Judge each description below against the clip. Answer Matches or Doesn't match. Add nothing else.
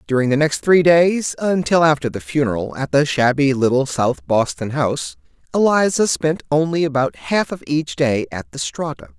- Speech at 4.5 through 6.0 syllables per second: Matches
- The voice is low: Doesn't match